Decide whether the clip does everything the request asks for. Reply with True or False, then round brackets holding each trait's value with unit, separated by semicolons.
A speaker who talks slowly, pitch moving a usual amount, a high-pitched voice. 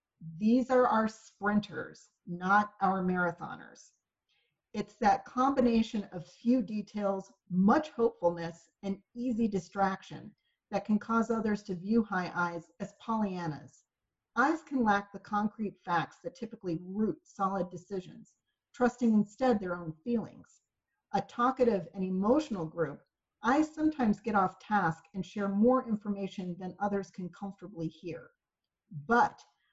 True (130 wpm; 4.0 semitones; 205 Hz)